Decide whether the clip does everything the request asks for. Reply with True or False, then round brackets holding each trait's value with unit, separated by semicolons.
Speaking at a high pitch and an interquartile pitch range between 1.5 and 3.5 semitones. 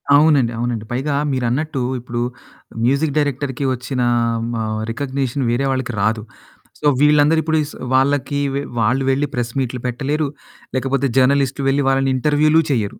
False (135 Hz; 2.9 semitones)